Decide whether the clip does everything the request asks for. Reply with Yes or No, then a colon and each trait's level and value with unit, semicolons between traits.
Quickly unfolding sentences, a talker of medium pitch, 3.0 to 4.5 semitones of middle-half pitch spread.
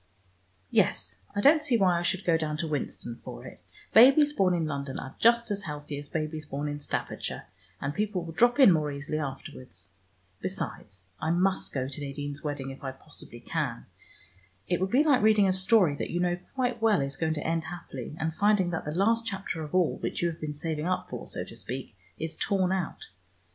No: fast, 210 wpm; medium, 165 Hz; average, 5.0 semitones